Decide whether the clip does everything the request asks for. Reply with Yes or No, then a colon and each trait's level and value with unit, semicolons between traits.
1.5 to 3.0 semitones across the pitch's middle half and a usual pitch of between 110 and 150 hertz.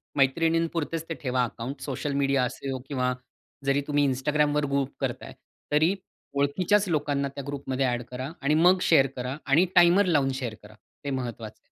Yes: average, 2.7 semitones; medium, 140 Hz